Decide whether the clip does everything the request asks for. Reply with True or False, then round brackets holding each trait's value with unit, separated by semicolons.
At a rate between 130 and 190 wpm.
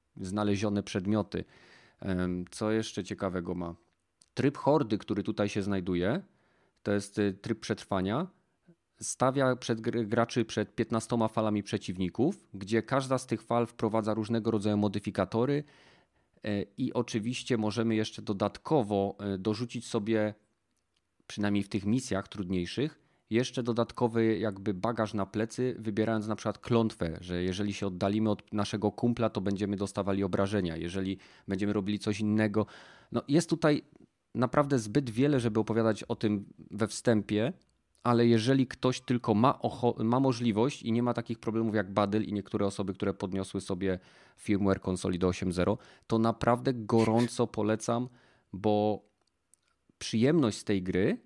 True (135 wpm)